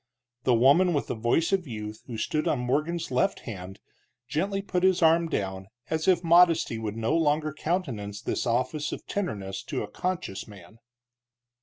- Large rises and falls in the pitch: Yes, wide, 7.5 semitones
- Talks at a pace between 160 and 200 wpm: Yes, average, 170 wpm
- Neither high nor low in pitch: Yes, medium, 145 Hz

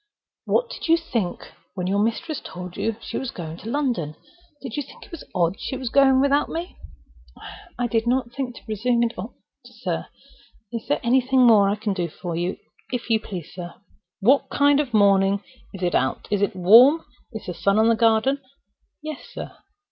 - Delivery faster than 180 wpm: Yes, average, 195 wpm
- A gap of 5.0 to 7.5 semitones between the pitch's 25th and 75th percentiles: Yes, average, 5.3 semitones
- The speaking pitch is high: Yes, high, 225 Hz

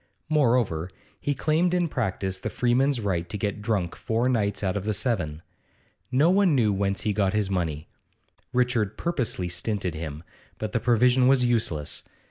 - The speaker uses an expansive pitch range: No, average, 4.9 semitones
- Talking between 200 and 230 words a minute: No, average, 165 wpm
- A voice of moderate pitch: No, low, 110 Hz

